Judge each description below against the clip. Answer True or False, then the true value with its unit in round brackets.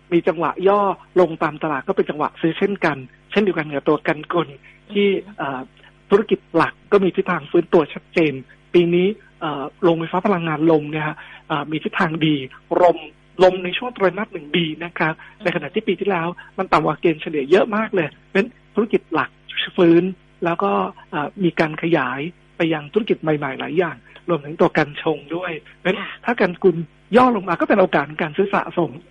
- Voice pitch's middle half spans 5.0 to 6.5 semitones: False (3.3 semitones)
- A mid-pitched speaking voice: True (175 Hz)